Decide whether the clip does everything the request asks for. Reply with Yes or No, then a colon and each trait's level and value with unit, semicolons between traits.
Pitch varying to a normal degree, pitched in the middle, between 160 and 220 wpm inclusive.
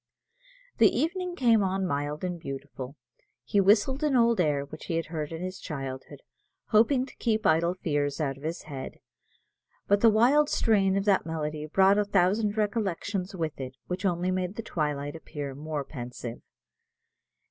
No: wide, 5.7 semitones; medium, 180 Hz; average, 170 wpm